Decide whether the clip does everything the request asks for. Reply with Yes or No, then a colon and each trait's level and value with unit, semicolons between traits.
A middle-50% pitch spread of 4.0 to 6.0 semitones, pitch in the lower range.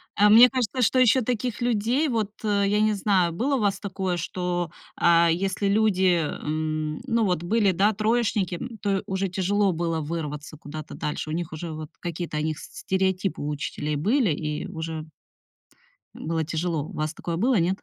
No: average, 4.6 semitones; medium, 185 Hz